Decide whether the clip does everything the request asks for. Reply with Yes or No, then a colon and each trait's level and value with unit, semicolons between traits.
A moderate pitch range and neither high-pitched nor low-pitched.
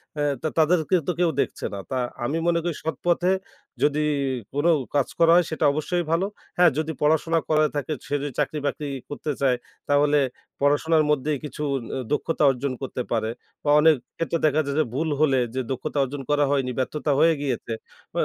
No: narrow, 2.2 semitones; medium, 150 Hz